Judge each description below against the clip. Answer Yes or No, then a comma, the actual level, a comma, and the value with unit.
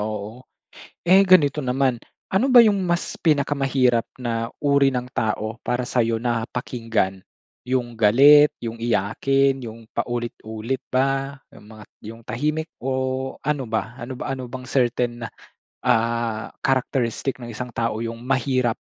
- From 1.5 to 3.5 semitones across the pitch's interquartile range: Yes, average, 2.9 semitones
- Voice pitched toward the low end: Yes, low, 125 Hz